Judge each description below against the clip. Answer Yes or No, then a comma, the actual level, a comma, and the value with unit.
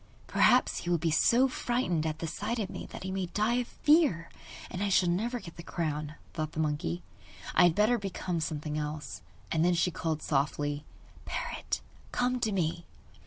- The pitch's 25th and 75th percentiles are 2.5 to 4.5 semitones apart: No, wide, 5.5 semitones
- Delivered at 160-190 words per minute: Yes, average, 185 wpm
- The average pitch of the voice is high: No, medium, 175 Hz